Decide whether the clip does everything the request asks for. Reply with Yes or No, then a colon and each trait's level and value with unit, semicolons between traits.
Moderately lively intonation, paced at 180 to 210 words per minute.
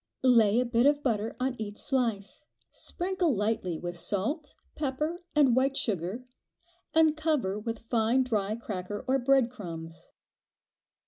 No: average, 4.7 semitones; slow, 135 wpm